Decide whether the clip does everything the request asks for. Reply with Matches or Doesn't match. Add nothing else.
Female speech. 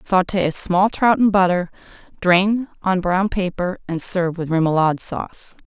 Matches